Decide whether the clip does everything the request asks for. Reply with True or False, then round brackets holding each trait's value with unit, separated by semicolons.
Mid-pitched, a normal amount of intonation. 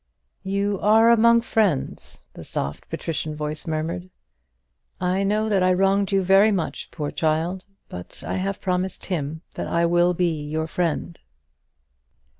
True (180 Hz; 3.7 semitones)